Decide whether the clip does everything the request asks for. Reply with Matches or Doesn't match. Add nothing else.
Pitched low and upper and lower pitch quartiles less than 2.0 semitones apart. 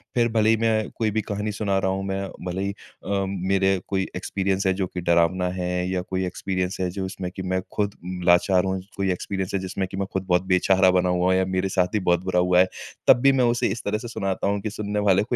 Matches